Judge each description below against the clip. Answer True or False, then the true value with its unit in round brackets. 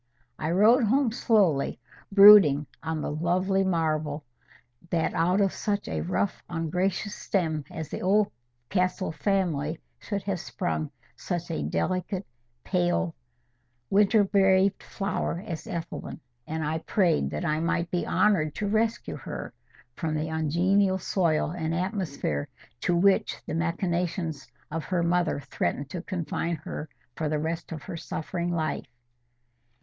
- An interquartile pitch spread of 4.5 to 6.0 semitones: False (3.4 semitones)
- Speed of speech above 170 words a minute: False (135 wpm)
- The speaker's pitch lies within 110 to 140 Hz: False (175 Hz)